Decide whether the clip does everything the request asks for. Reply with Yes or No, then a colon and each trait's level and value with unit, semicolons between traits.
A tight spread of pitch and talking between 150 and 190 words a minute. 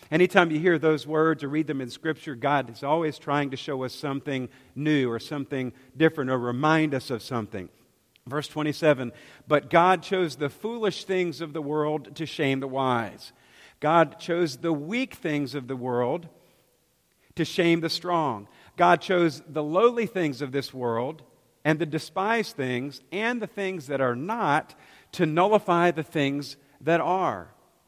No: average, 3.7 semitones; average, 170 wpm